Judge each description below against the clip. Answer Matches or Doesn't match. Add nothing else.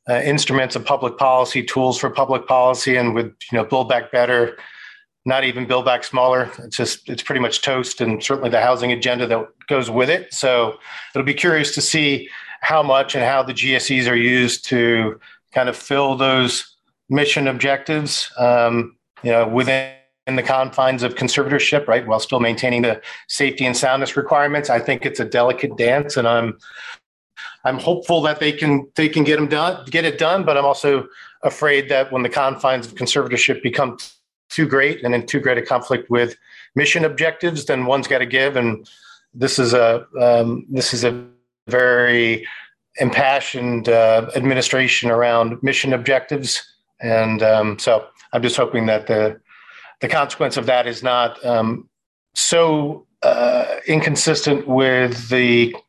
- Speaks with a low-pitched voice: Matches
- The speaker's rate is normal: Matches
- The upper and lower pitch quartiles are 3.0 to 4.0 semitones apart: Doesn't match